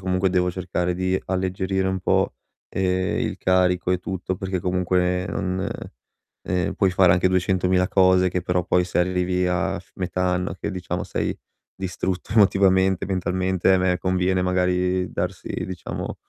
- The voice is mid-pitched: No, very low, 90 Hz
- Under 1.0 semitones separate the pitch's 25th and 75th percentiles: Yes, narrow, 0.6 semitones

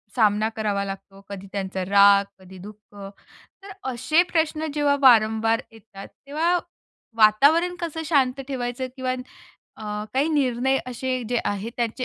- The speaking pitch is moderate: No, high, 240 Hz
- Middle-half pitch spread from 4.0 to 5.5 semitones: Yes, average, 5.1 semitones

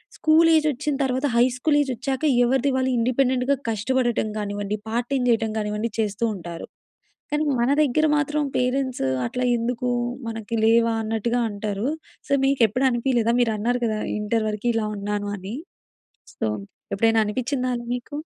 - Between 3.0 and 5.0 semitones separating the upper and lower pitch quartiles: Yes, average, 3.3 semitones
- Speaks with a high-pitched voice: Yes, high, 240 Hz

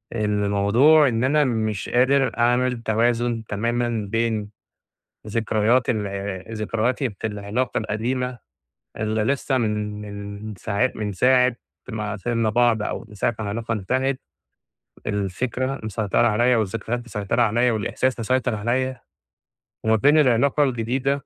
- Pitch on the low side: Yes, low, 115 Hz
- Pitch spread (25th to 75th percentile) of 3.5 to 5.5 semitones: No, average, 3.0 semitones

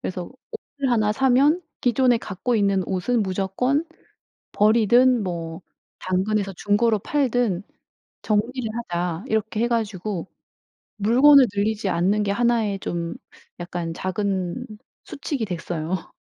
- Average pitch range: Yes, average, 4.5 semitones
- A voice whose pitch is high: Yes, high, 210 Hz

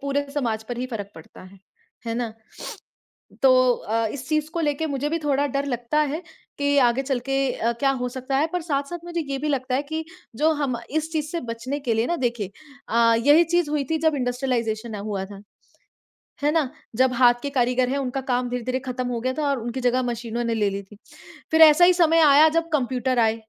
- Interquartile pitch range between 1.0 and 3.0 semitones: No, average, 3.6 semitones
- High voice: Yes, very high, 260 Hz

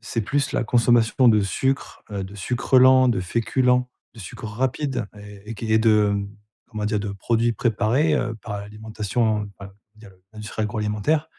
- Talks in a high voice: No, low, 110 Hz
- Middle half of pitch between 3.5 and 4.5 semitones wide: No, average, 3.0 semitones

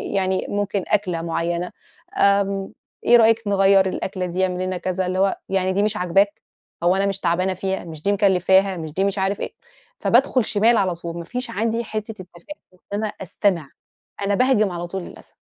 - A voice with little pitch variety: Yes, narrow, 2.1 semitones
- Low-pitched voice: No, high, 190 Hz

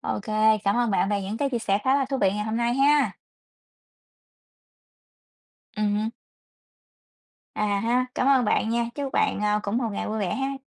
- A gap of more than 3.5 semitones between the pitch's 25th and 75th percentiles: Yes, average, 4.0 semitones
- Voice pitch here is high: Yes, high, 225 Hz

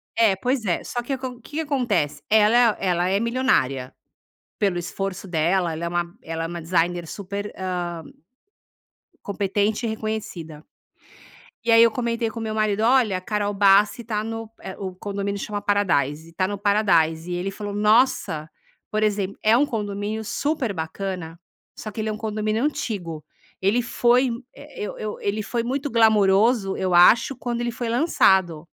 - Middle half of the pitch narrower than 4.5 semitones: Yes, average, 4.0 semitones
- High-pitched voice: Yes, high, 205 Hz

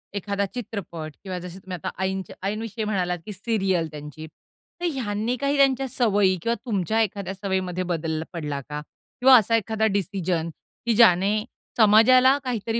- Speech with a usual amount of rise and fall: Yes, average, 4.0 semitones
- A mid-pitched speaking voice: No, high, 200 Hz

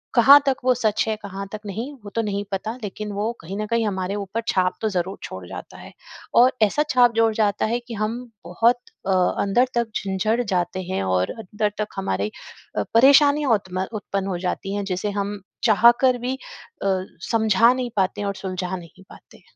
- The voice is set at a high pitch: Yes, high, 205 Hz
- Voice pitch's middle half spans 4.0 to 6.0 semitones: No, average, 3.4 semitones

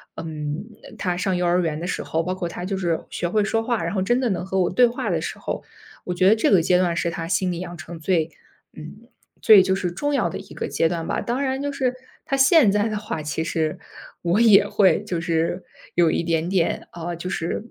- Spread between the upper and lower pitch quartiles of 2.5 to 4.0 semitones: Yes, average, 3.7 semitones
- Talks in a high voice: No, medium, 180 Hz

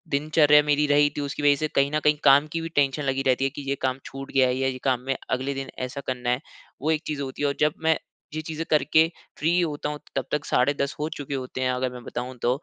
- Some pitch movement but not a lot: No, narrow, 2.2 semitones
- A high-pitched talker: No, medium, 140 Hz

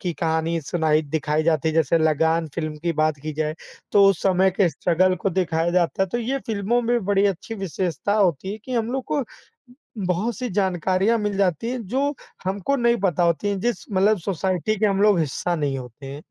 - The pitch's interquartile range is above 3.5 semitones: Yes, average, 4.2 semitones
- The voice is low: No, medium, 185 Hz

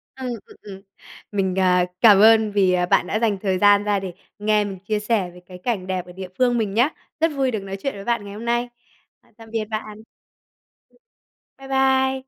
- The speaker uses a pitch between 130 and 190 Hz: No, high, 210 Hz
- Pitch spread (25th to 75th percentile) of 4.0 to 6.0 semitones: No, average, 3.5 semitones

